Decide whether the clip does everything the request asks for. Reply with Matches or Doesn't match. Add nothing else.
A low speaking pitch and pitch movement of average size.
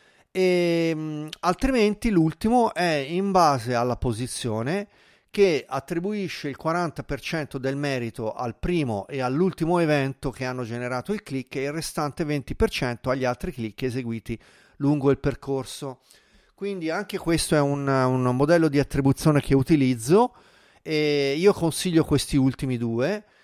Doesn't match